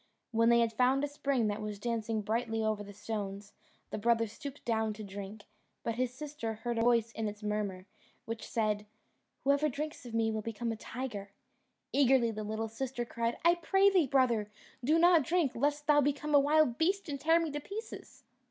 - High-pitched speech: Yes, high, 235 Hz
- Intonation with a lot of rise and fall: No, average, 4.7 semitones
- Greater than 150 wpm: Yes, average, 200 wpm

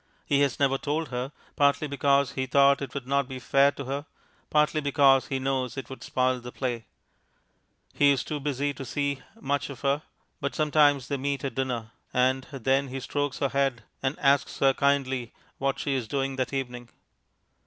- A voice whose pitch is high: No, low, 135 Hz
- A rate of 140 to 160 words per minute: No, average, 190 wpm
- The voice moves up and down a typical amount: No, narrow, 1.4 semitones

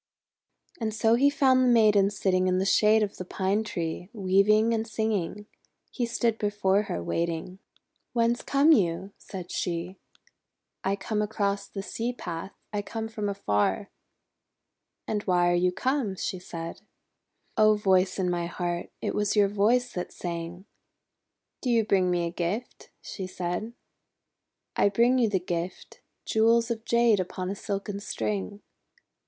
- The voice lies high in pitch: Yes, high, 200 Hz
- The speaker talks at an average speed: Yes, average, 160 wpm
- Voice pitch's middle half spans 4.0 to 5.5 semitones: No, average, 3.6 semitones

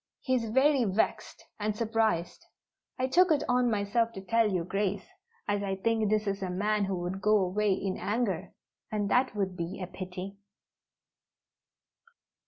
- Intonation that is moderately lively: Yes, average, 3.1 semitones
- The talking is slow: No, average, 165 wpm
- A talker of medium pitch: No, high, 205 Hz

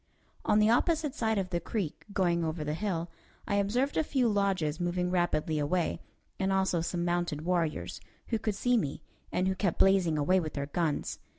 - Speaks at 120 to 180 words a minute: No, average, 190 wpm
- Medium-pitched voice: Yes, medium, 180 Hz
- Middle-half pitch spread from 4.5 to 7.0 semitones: No, average, 3.7 semitones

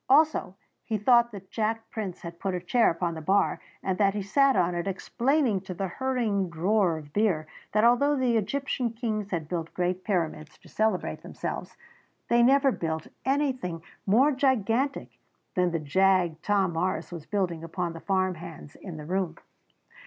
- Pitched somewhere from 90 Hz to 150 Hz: No, high, 195 Hz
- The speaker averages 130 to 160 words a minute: No, average, 175 wpm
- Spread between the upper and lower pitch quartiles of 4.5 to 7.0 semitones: Yes, average, 5.3 semitones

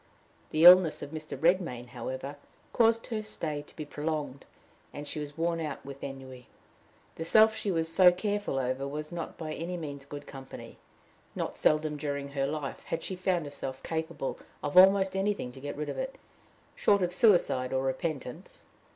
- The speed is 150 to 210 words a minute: Yes, average, 175 wpm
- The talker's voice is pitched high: No, medium, 155 Hz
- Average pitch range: Yes, average, 4.3 semitones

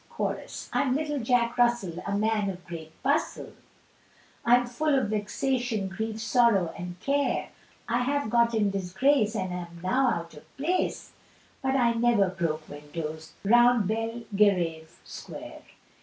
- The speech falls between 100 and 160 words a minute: Yes, average, 145 wpm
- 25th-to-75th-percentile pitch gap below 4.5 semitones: No, average, 5.2 semitones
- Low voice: No, high, 220 Hz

